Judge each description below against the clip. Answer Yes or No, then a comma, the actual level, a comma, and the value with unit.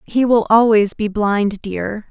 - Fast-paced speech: No, average, 170 wpm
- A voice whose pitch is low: No, high, 215 Hz